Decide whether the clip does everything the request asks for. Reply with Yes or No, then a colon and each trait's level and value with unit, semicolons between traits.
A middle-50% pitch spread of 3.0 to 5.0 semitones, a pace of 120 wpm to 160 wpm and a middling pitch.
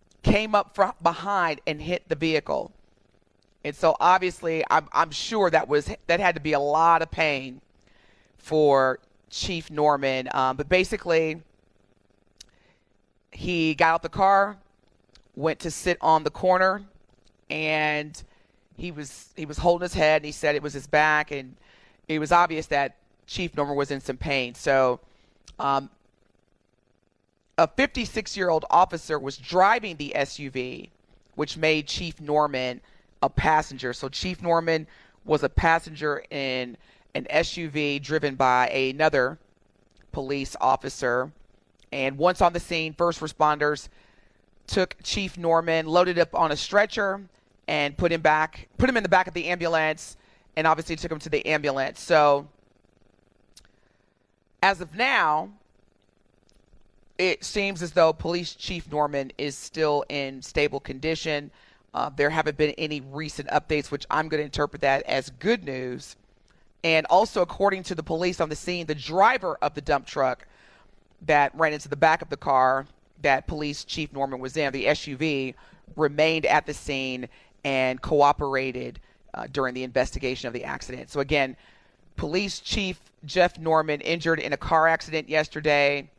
Yes: average, 4.0 semitones; average, 155 wpm; medium, 150 Hz